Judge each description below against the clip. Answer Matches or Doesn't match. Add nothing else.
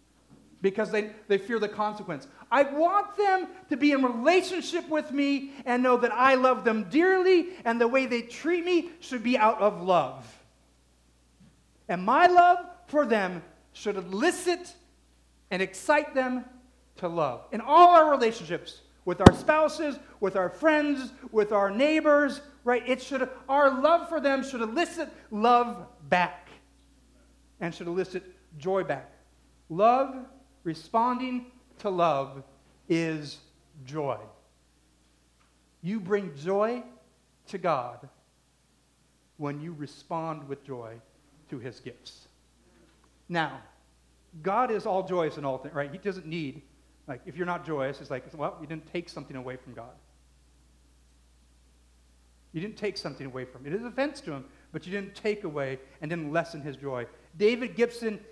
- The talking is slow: Doesn't match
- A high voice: Matches